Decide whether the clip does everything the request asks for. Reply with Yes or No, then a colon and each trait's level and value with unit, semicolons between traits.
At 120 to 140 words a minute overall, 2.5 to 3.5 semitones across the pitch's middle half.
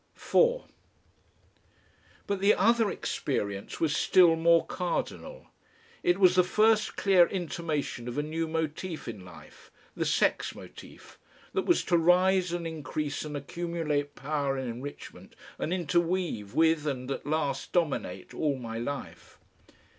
No: slow, 135 wpm; average, 4.0 semitones